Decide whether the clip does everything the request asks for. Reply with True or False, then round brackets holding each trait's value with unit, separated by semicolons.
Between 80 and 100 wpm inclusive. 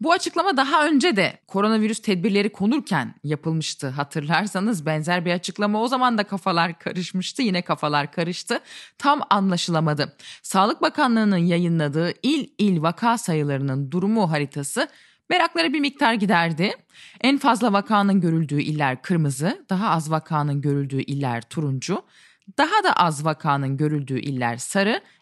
False (130 wpm)